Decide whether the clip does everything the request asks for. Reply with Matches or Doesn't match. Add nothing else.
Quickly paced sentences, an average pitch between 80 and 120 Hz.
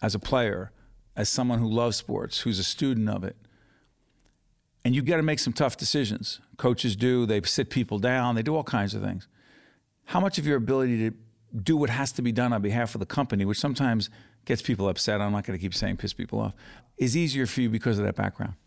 Matches